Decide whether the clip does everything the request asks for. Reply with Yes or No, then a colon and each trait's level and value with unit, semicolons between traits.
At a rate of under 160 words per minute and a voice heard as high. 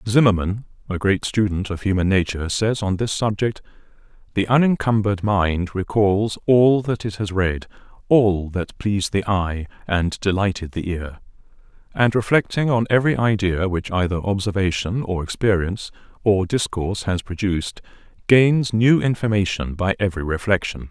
No: average, 140 wpm; low, 100 Hz